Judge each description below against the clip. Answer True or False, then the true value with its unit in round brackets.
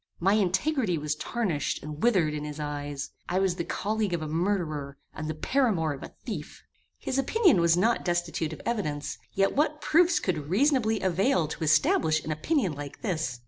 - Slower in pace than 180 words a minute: False (185 wpm)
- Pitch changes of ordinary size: False (6.3 semitones)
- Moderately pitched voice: True (175 Hz)